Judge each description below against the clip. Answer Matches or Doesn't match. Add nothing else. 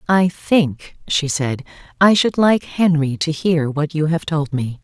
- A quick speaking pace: Doesn't match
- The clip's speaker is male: Doesn't match